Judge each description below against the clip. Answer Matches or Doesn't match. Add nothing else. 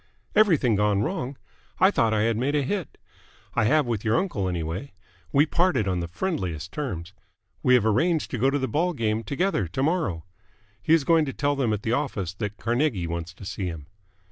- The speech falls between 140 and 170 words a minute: Doesn't match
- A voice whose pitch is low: Matches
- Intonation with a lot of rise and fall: Matches